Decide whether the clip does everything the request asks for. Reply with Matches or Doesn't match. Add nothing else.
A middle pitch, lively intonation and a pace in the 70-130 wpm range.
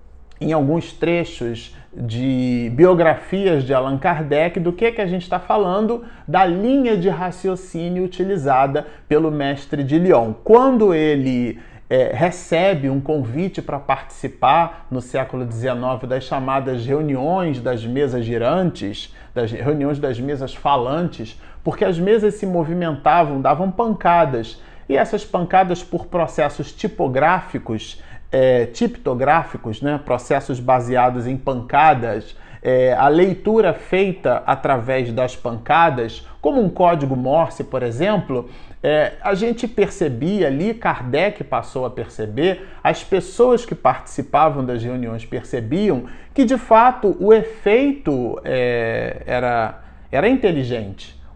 Matches